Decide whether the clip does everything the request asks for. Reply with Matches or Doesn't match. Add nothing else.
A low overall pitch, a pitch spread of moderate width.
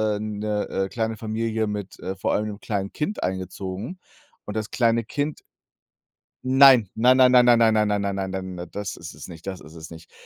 Matches